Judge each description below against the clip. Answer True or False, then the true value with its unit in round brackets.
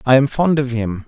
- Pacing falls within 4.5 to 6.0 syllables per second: True (5.3 syllables/s)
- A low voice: True (130 Hz)